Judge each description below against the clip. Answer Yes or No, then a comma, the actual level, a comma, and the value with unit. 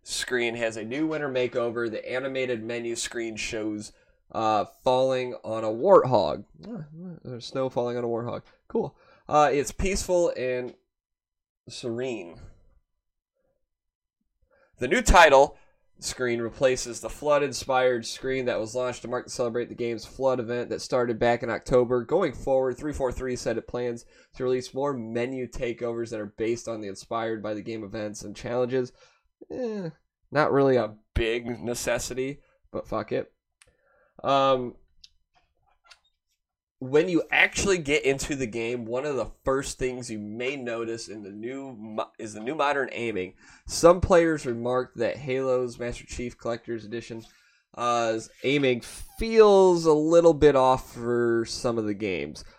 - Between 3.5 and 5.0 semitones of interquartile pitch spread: No, narrow, 2.5 semitones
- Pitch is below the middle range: Yes, low, 120 Hz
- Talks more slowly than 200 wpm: Yes, average, 150 wpm